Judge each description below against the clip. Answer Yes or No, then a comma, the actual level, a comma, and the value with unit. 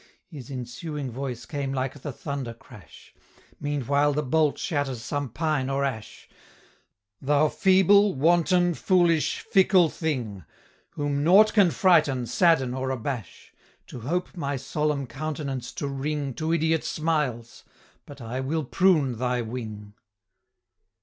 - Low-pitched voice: No, medium, 145 Hz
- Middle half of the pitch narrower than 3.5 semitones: No, average, 3.8 semitones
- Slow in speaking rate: Yes, slow, 130 wpm